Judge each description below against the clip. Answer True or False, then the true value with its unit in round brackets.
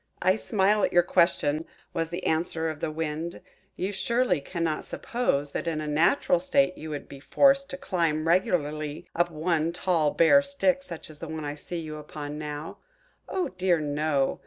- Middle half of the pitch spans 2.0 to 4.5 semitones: True (3.6 semitones)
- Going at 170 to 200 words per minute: True (175 wpm)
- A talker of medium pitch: True (165 Hz)